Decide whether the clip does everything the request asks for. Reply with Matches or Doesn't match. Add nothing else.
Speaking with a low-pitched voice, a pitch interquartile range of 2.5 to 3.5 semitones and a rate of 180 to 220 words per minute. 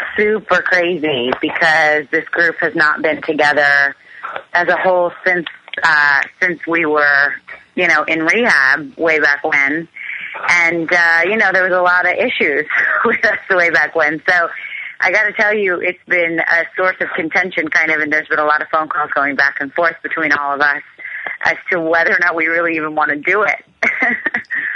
Doesn't match